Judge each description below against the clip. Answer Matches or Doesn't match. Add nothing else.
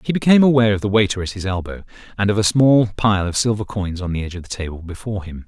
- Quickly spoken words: Matches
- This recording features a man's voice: Matches